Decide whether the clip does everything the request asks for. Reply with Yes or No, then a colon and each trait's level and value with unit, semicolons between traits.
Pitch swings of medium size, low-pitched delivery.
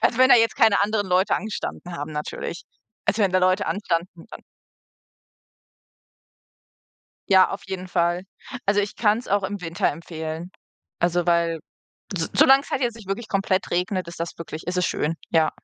No: average, 3.3 semitones; medium, 185 Hz